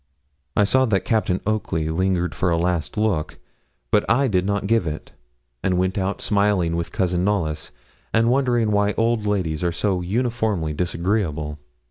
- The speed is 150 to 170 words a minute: Yes, average, 160 wpm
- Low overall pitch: Yes, very low, 95 Hz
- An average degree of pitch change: Yes, average, 3.9 semitones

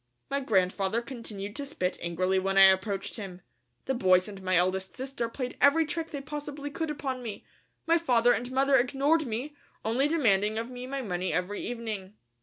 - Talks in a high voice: Yes, high, 235 Hz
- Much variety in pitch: Yes, wide, 6.1 semitones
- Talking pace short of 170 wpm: No, average, 185 wpm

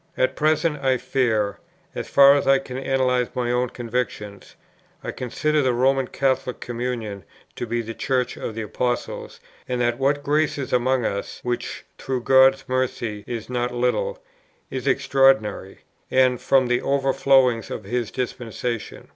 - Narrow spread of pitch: Yes, narrow, 2.0 semitones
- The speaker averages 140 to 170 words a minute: Yes, average, 155 wpm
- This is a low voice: Yes, low, 125 Hz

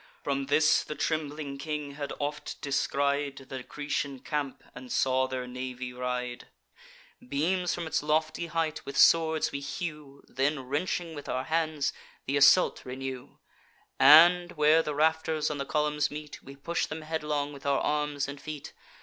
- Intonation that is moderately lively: No, narrow, 2.2 semitones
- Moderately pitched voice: Yes, medium, 145 Hz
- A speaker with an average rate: Yes, average, 160 wpm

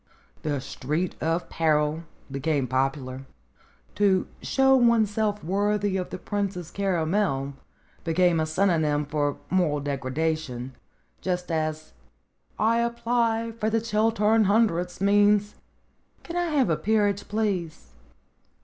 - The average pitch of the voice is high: No, medium, 180 Hz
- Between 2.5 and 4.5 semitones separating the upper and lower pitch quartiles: No, average, 5.3 semitones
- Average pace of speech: No, slow, 115 wpm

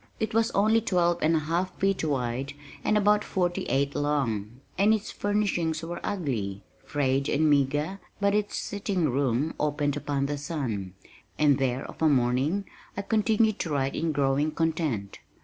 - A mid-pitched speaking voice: Yes, medium, 150 Hz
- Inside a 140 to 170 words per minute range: Yes, average, 165 wpm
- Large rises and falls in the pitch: Yes, wide, 6.2 semitones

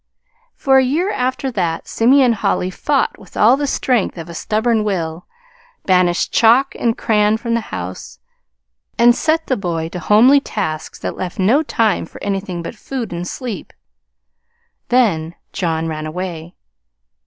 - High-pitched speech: Yes, high, 210 Hz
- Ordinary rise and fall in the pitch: No, wide, 6.4 semitones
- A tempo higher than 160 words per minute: No, average, 155 wpm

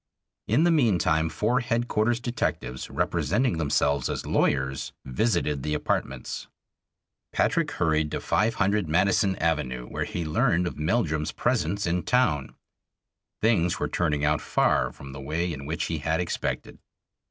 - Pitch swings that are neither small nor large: No, wide, 6.2 semitones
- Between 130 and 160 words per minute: Yes, average, 140 wpm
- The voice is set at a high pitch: No, very low, 80 Hz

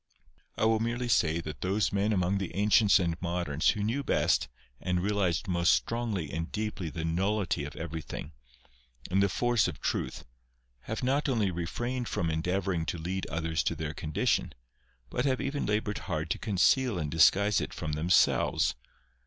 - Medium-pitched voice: No, very low, 95 Hz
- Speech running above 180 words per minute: No, average, 170 wpm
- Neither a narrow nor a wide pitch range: Yes, average, 4.7 semitones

